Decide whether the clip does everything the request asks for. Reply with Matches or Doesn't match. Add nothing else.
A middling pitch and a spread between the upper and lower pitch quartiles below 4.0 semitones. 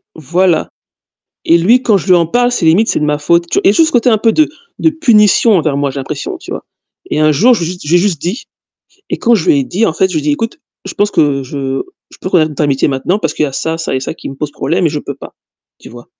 Doesn't match